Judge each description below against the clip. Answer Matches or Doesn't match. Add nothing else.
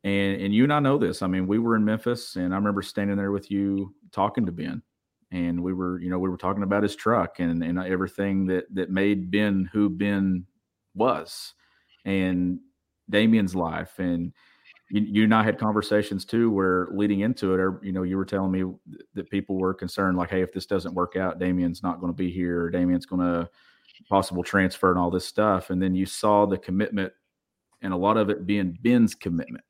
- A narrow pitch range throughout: Matches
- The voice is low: Matches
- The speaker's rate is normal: Doesn't match